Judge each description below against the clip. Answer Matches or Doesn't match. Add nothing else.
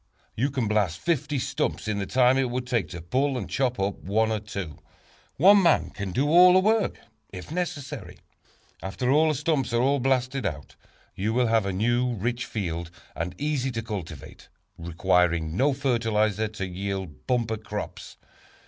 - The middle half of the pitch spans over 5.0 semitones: Matches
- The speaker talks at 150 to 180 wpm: Matches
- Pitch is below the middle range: Matches